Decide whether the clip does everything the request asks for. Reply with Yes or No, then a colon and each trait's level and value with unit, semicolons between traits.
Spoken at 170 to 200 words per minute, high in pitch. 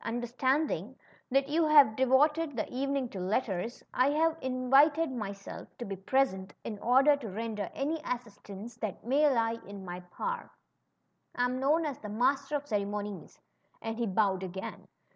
No: average, 160 wpm; high, 245 Hz